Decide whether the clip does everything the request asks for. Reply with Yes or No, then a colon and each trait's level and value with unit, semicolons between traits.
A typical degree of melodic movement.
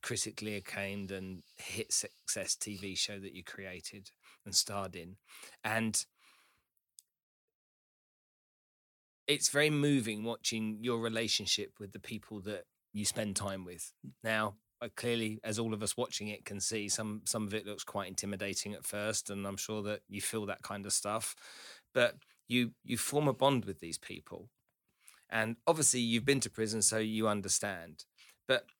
No: narrow, 2.2 semitones